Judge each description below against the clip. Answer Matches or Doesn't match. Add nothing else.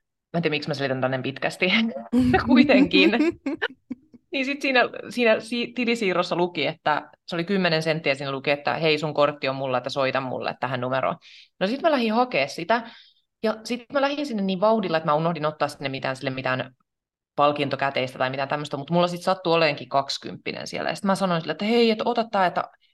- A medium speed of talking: Doesn't match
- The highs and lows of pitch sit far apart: Matches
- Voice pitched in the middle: Matches